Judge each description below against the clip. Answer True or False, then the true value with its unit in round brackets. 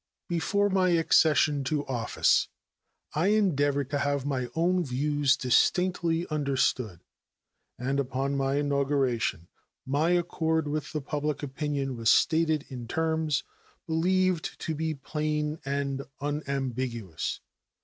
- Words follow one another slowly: True (115 wpm)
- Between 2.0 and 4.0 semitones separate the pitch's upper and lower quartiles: True (3.0 semitones)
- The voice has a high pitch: False (145 Hz)